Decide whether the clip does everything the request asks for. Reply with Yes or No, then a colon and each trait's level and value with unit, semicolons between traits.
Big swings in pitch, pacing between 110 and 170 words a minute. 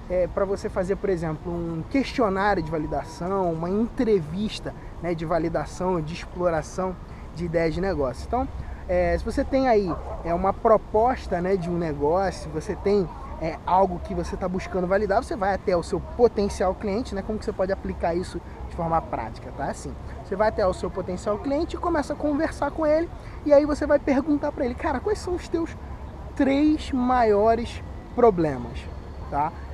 No: wide, 5.8 semitones; average, 185 wpm